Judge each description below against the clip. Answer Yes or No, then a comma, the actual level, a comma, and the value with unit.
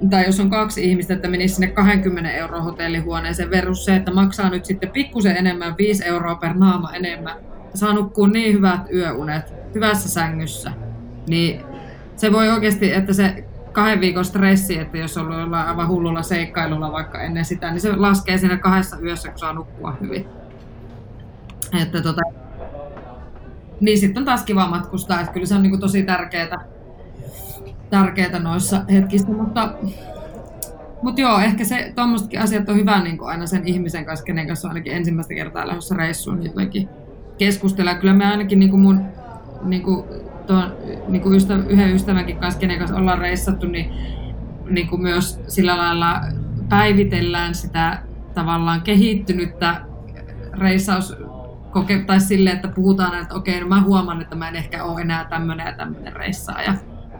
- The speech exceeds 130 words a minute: Yes, fast, 155 wpm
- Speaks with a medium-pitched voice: Yes, medium, 180 Hz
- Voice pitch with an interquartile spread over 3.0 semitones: No, average, 2.7 semitones